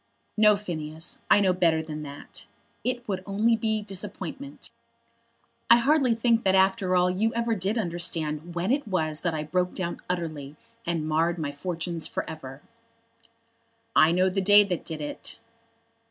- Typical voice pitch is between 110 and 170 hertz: No, medium, 180 Hz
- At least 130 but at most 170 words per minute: Yes, average, 160 wpm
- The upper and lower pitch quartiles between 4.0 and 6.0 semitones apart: Yes, average, 4.6 semitones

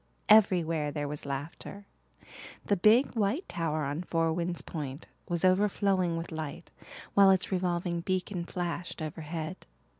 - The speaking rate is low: Yes, slow, 130 wpm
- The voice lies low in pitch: No, medium, 175 Hz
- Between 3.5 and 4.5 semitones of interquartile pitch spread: No, average, 3.1 semitones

